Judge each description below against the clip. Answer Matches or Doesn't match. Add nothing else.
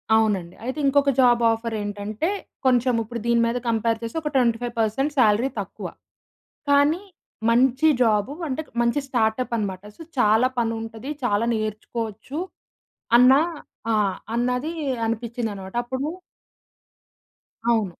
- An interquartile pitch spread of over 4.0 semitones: Doesn't match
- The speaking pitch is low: Doesn't match